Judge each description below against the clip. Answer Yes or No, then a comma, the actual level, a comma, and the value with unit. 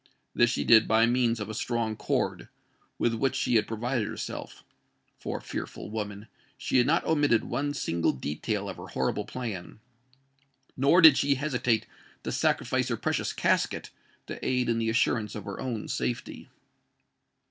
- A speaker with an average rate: Yes, average, 150 wpm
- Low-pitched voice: Yes, low, 120 Hz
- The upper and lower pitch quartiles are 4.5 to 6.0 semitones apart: No, average, 3.3 semitones